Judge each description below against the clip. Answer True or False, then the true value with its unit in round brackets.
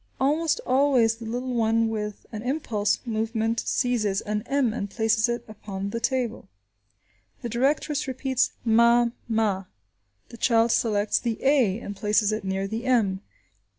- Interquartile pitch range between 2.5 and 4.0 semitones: True (2.8 semitones)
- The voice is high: True (225 Hz)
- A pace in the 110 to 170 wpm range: True (145 wpm)